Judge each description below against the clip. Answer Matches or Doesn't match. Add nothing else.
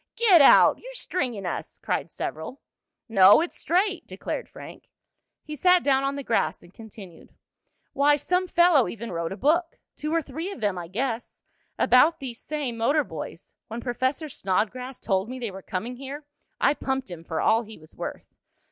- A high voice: Matches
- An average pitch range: Doesn't match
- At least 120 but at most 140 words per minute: Doesn't match